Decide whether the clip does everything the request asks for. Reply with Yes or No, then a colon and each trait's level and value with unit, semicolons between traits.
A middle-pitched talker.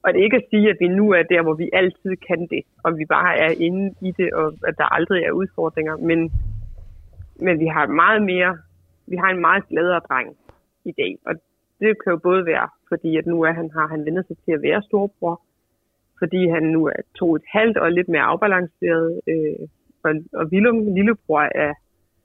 Yes: medium, 165 Hz